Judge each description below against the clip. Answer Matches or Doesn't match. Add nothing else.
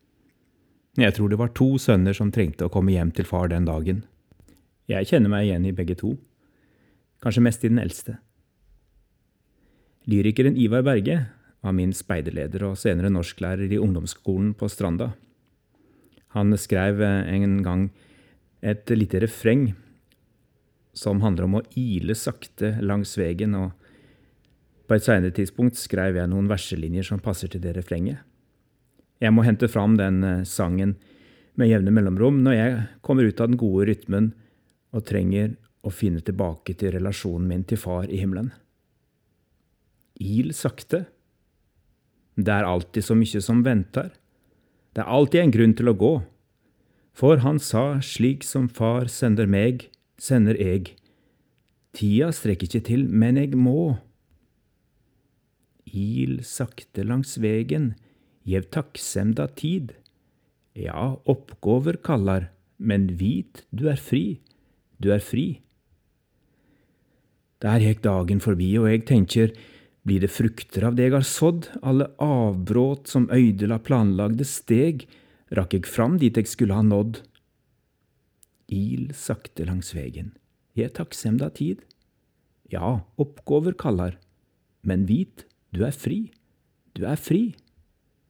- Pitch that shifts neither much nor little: Matches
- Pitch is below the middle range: Matches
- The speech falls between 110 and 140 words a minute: Matches